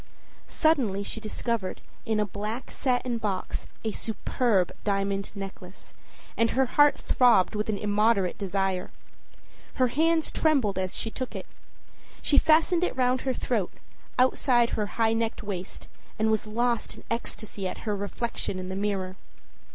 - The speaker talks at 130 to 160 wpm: Yes, average, 150 wpm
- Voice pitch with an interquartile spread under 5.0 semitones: Yes, average, 3.9 semitones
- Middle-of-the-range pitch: No, high, 220 Hz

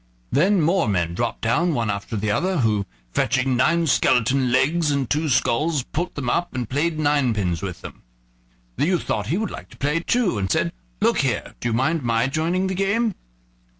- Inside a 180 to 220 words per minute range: Yes, average, 195 wpm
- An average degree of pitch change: No, wide, 6.7 semitones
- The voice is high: No, medium, 140 Hz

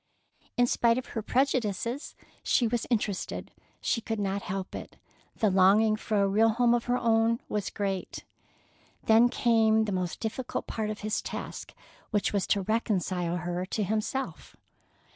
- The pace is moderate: Yes, average, 160 wpm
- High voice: Yes, high, 220 Hz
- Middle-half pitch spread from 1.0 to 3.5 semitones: Yes, average, 2.8 semitones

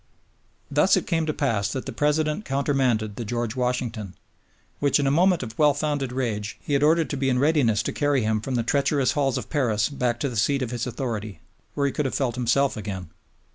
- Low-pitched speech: Yes, low, 130 Hz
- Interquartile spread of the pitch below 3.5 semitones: No, average, 4.1 semitones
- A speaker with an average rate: No, fast, 220 wpm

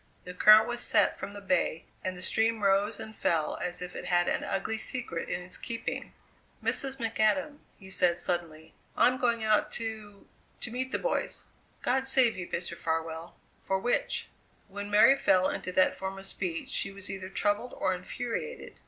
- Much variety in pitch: No, average, 4.1 semitones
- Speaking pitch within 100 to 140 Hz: No, high, 200 Hz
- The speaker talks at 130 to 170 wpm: No, average, 180 wpm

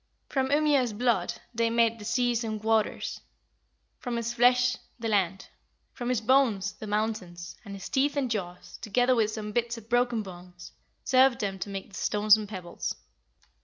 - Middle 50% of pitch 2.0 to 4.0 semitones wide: Yes, average, 3.1 semitones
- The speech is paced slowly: No, average, 170 wpm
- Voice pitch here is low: No, high, 225 Hz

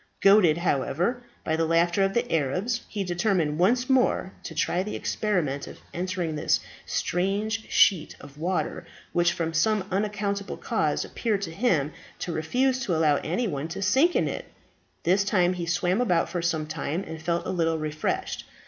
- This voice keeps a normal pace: Yes, average, 170 wpm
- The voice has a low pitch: No, medium, 180 Hz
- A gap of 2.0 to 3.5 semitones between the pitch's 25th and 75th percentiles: No, average, 4.2 semitones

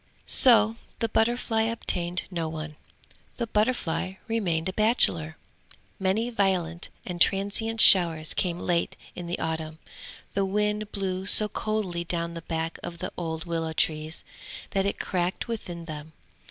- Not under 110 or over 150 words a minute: Yes, average, 140 wpm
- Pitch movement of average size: Yes, average, 4.3 semitones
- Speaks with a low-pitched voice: No, medium, 180 Hz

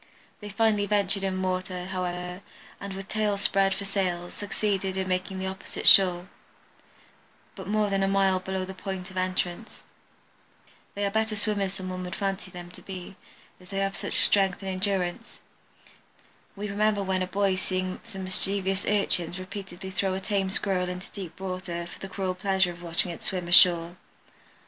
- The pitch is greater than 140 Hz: Yes, high, 190 Hz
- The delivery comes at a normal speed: Yes, average, 180 wpm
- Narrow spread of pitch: Yes, narrow, 1.4 semitones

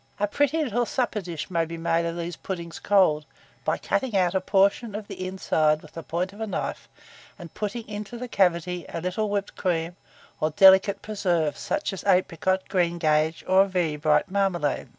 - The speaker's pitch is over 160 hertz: Yes, medium, 185 Hz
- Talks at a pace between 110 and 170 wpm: No, average, 185 wpm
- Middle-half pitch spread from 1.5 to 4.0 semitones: Yes, average, 3.4 semitones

